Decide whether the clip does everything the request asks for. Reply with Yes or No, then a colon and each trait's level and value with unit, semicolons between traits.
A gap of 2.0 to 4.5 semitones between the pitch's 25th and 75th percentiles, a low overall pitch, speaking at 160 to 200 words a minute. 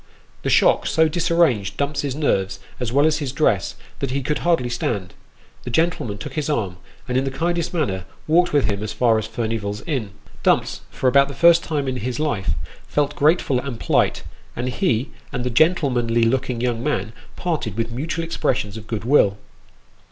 No: average, 5.0 semitones; low, 130 Hz; average, 185 wpm